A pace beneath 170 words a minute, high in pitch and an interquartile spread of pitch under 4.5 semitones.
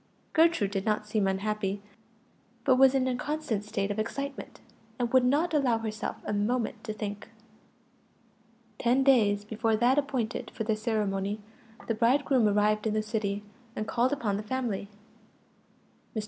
Yes: average, 155 wpm; high, 220 Hz; average, 3.5 semitones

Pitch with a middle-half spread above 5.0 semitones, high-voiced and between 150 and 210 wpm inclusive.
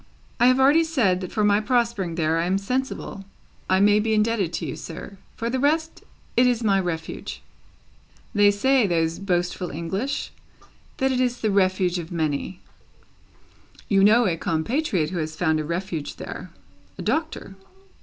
Yes: wide, 5.6 semitones; high, 195 Hz; average, 165 wpm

